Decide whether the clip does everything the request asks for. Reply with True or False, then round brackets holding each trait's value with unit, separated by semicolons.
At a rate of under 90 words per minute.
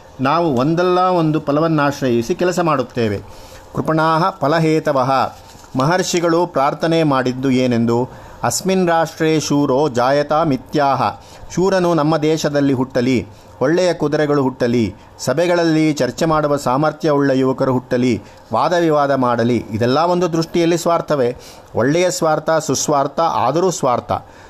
False (105 wpm)